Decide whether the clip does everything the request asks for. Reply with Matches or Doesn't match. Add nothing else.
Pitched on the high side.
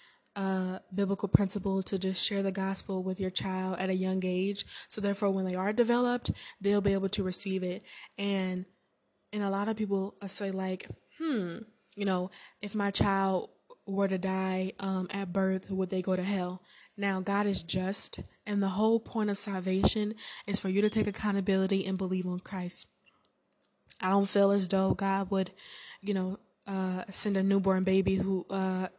Matches